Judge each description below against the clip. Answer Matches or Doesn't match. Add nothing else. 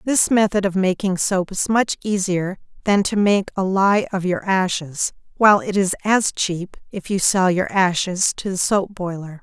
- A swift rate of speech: Doesn't match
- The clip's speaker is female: Matches